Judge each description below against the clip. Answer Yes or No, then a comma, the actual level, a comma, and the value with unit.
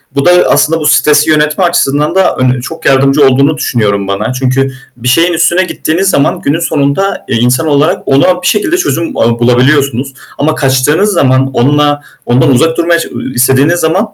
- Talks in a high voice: No, medium, 145 Hz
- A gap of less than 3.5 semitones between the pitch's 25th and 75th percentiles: No, average, 3.9 semitones